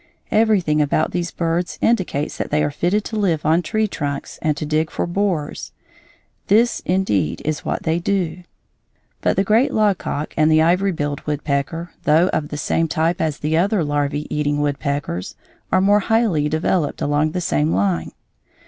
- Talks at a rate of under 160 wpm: No, average, 170 wpm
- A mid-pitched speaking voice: Yes, medium, 160 Hz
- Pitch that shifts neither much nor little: Yes, average, 4.1 semitones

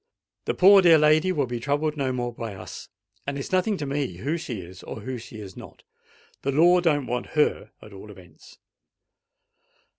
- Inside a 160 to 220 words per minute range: Yes, average, 190 wpm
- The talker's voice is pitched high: No, medium, 140 Hz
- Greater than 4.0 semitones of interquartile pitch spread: Yes, average, 5.0 semitones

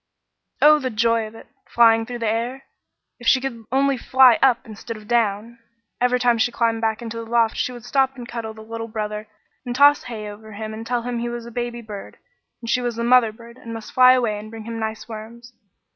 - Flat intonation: Yes, narrow, 1.9 semitones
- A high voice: Yes, high, 230 Hz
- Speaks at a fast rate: Yes, fast, 235 wpm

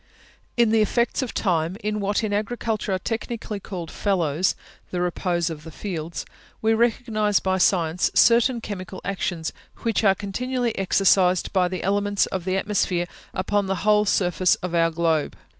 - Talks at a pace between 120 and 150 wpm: No, average, 160 wpm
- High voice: Yes, high, 195 Hz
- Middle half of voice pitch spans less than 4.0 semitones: Yes, average, 3.2 semitones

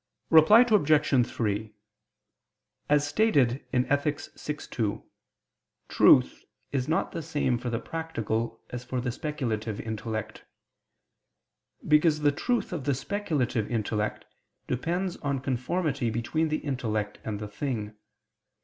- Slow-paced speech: Yes, slow, 120 wpm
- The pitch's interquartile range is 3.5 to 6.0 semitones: Yes, average, 5.2 semitones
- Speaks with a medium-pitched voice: No, low, 130 Hz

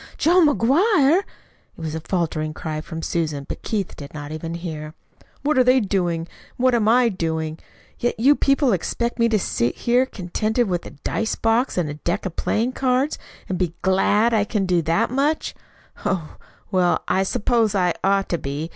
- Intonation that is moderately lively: No, wide, 6.7 semitones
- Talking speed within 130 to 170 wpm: No, average, 190 wpm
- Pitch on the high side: Yes, high, 195 Hz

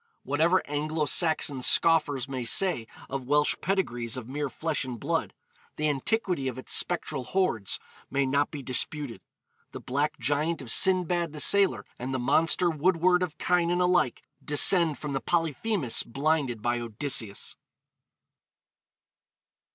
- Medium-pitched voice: Yes, medium, 150 Hz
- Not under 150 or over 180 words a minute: No, slow, 135 wpm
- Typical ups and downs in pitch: Yes, average, 4.5 semitones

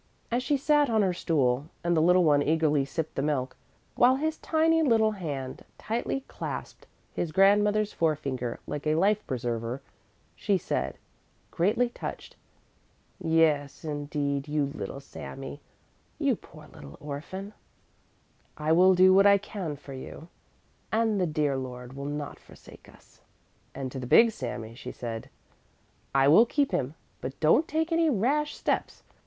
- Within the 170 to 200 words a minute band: No, average, 150 wpm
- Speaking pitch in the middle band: Yes, medium, 160 Hz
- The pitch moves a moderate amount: No, wide, 7.2 semitones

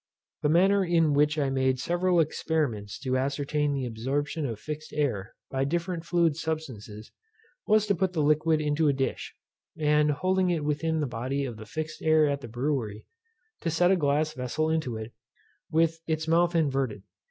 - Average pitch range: Yes, average, 3.5 semitones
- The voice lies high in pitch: No, medium, 150 Hz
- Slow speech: No, average, 175 wpm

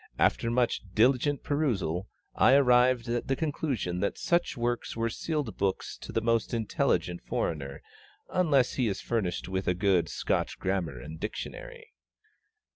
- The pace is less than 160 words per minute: Yes, average, 145 wpm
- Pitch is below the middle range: Yes, low, 115 Hz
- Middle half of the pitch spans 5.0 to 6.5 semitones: Yes, wide, 5.5 semitones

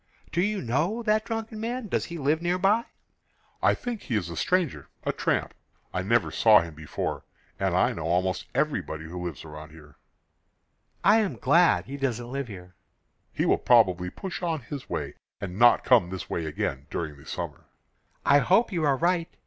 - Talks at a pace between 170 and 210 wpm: Yes, average, 185 wpm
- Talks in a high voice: No, low, 130 Hz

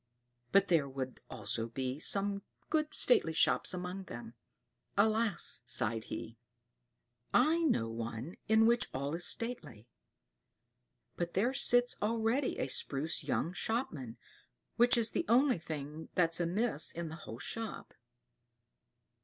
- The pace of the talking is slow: Yes, slow, 130 wpm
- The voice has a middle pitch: Yes, medium, 175 Hz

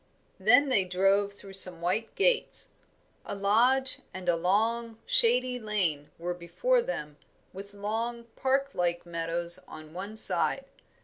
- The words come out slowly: Yes, slow, 130 wpm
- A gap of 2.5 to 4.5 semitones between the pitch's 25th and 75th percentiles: No, average, 5.0 semitones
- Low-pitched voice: No, high, 200 Hz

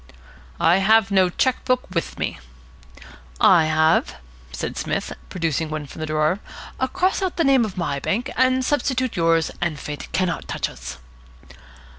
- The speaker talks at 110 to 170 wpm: Yes, average, 150 wpm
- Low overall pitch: No, medium, 180 Hz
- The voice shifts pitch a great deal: Yes, wide, 7.7 semitones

